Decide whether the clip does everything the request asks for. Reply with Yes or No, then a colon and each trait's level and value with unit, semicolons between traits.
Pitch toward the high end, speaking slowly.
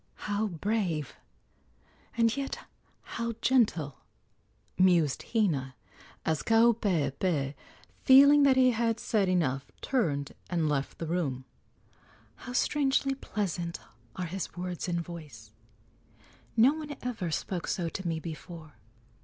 No: medium, 180 Hz; slow, 115 wpm